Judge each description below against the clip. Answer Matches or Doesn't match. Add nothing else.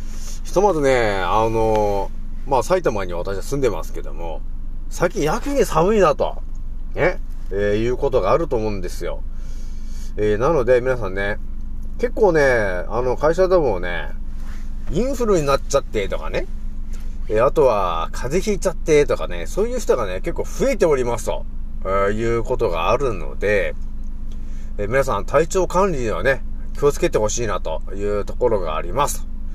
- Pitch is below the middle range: Matches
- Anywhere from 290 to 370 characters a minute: Matches